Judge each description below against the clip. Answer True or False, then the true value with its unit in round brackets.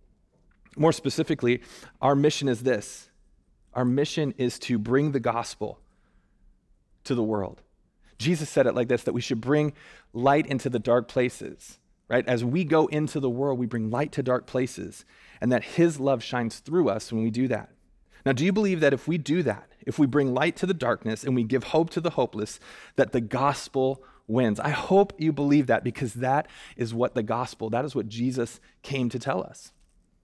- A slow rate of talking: False (200 wpm)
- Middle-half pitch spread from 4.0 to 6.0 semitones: False (3.3 semitones)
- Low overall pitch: True (130 Hz)